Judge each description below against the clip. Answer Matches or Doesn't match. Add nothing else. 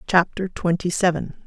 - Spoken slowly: Matches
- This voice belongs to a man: Doesn't match